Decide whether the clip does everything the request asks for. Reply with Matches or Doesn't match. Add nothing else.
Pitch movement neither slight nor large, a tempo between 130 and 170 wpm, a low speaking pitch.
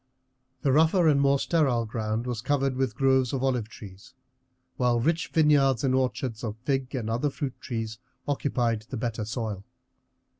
Matches